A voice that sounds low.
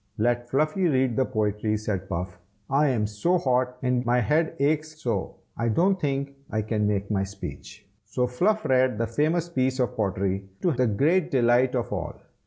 Yes: low, 125 Hz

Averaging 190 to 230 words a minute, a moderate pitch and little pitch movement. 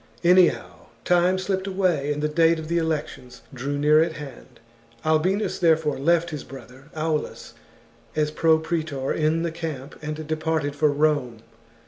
No: average, 155 wpm; medium, 155 Hz; narrow, 2.3 semitones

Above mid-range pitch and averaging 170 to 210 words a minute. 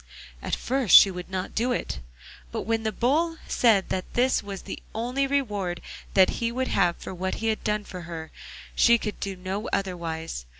Yes: high, 205 Hz; average, 195 wpm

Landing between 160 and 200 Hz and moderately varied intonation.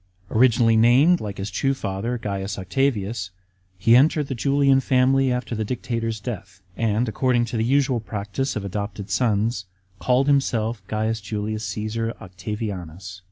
No: low, 115 Hz; average, 3.8 semitones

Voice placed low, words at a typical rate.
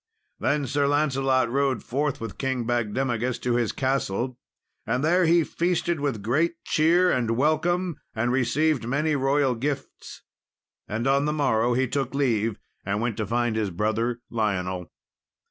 Yes: low, 130 Hz; average, 155 wpm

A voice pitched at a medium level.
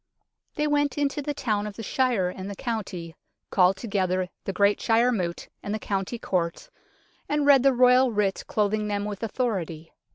No: high, 210 Hz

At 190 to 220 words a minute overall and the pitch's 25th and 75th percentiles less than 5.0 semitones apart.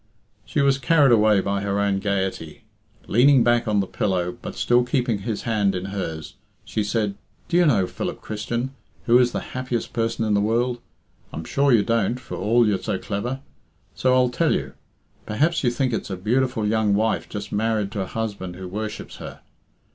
Yes: average, 195 wpm; average, 3.6 semitones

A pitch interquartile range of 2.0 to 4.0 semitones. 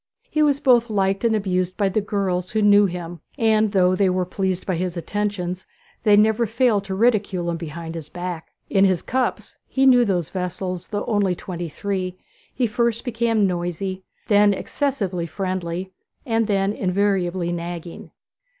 Yes: average, 3.1 semitones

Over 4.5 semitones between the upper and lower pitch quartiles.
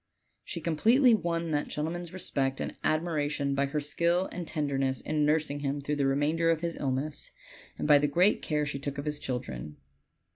No: average, 3.0 semitones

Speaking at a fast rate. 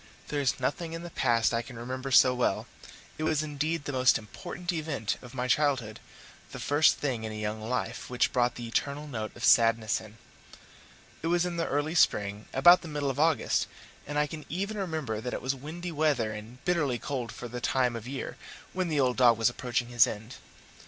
Yes: fast, 210 wpm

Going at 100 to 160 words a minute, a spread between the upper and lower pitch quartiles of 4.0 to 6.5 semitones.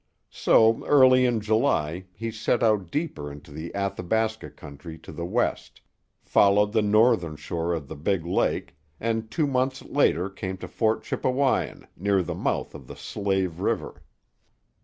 Yes: average, 155 wpm; average, 5.2 semitones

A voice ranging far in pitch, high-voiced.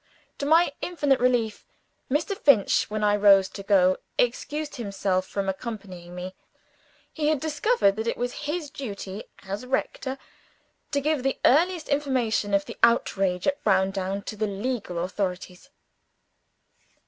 Yes: wide, 6.4 semitones; high, 220 Hz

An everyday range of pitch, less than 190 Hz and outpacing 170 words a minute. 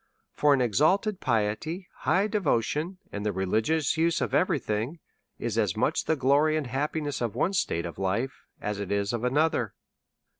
No: wide, 7.0 semitones; low, 135 Hz; average, 180 wpm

